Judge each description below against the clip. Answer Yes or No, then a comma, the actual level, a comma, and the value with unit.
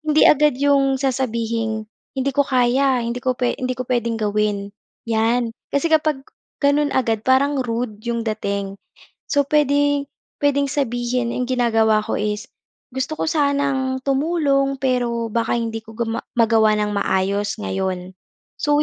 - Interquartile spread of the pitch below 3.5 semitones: No, average, 3.8 semitones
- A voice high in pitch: Yes, high, 245 Hz